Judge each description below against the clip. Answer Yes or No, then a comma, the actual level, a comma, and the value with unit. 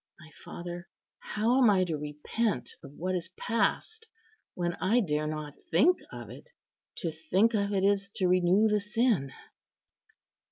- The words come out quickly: No, average, 155 wpm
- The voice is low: No, medium, 185 Hz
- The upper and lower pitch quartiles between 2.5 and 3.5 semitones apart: No, average, 5.1 semitones